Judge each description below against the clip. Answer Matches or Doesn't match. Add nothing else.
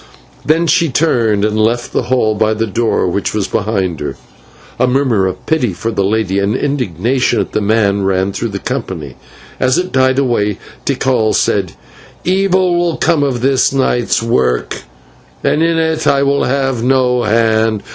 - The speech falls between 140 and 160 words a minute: Doesn't match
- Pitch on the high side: Doesn't match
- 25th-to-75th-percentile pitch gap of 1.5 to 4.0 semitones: Doesn't match